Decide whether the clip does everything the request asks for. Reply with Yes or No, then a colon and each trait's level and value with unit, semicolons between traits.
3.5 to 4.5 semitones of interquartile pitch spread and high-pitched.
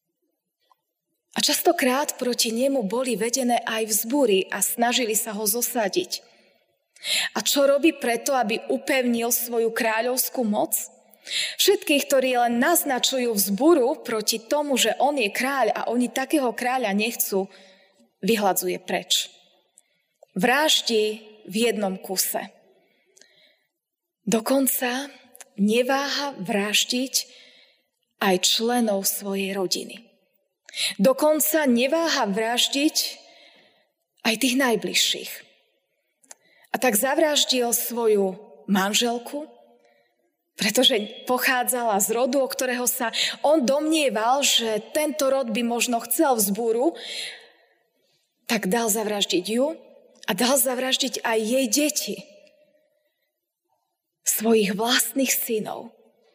Yes: average, 3.8 semitones; high, 245 Hz